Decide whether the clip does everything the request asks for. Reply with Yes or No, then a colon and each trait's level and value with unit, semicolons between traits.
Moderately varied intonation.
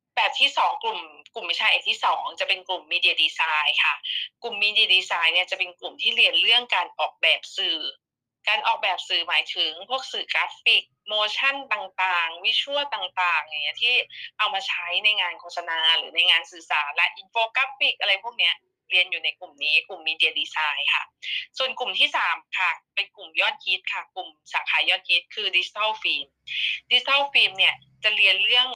No: wide, 6.4 semitones